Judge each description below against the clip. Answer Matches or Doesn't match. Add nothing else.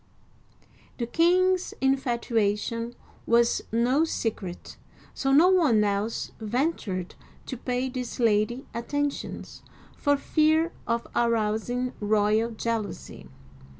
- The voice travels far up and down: Doesn't match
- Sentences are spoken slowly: Matches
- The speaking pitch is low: Doesn't match